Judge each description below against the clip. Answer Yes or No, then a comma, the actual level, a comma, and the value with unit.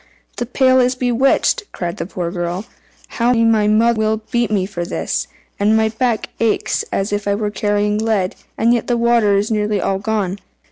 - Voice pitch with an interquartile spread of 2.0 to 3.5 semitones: Yes, narrow, 2.6 semitones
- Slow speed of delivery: No, average, 190 wpm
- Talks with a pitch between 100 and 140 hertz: No, high, 215 Hz